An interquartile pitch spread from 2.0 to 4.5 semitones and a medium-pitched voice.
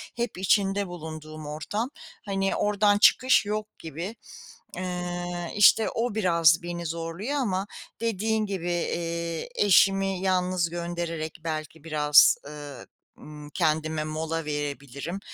Yes: average, 3.8 semitones; medium, 175 Hz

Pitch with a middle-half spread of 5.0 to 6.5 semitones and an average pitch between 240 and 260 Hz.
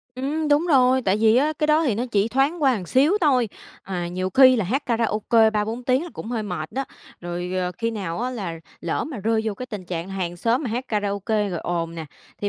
No: wide, 5.5 semitones; high, 225 Hz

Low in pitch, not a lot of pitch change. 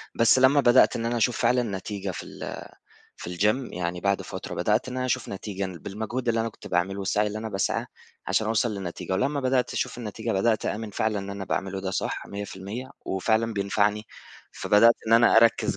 No: low, 105 Hz; average, 3.1 semitones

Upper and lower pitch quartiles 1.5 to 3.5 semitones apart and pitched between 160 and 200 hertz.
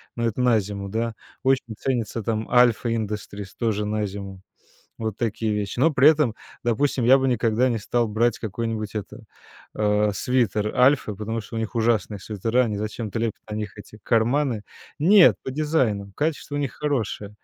No: average, 2.9 semitones; low, 115 Hz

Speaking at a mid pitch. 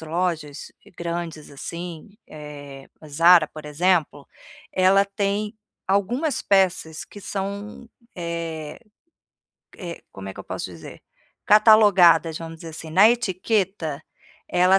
Yes: medium, 175 Hz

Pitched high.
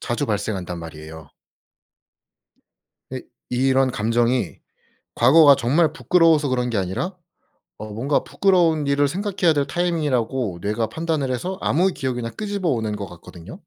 No: low, 130 Hz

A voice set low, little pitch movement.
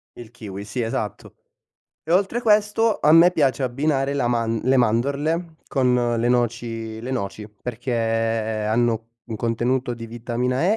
No: low, 120 Hz; average, 3.4 semitones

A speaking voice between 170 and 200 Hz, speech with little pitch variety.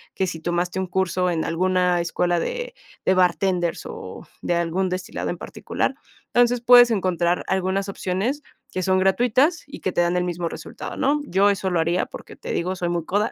Yes: medium, 185 Hz; narrow, 2.2 semitones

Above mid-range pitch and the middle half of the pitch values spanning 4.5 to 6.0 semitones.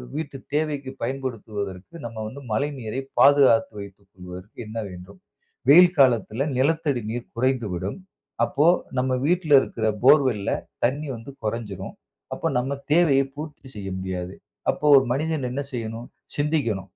No: low, 125 Hz; average, 5.2 semitones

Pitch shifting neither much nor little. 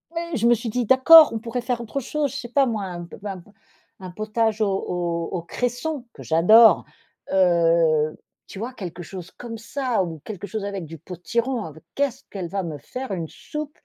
No: wide, 5.9 semitones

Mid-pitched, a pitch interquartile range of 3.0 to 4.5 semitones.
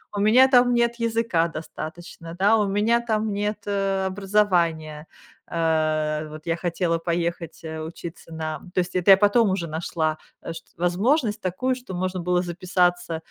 Yes: medium, 180 Hz; average, 4.0 semitones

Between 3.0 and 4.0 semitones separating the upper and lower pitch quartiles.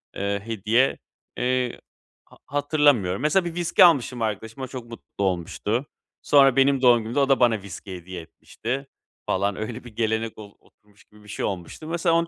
No: average, 4.8 semitones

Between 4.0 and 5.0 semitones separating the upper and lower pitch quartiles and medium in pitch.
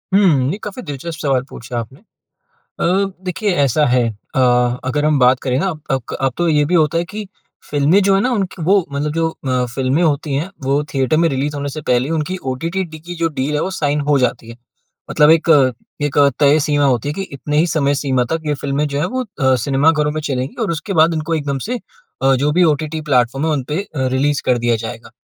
No: average, 3.5 semitones; medium, 145 Hz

